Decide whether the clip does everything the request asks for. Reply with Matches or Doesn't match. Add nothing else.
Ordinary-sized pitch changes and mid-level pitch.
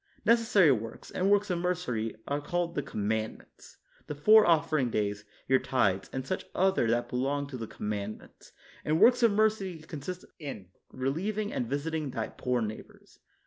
Doesn't match